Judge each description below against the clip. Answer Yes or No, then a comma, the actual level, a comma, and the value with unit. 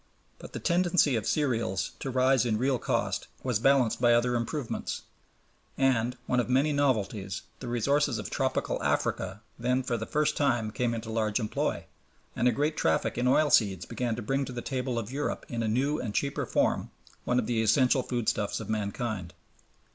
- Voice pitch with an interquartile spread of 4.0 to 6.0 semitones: No, average, 3.2 semitones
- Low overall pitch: Yes, low, 120 Hz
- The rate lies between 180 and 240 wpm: Yes, average, 185 wpm